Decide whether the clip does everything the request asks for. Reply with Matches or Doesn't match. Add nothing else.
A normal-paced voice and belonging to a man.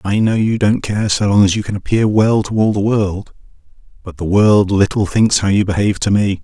Doesn't match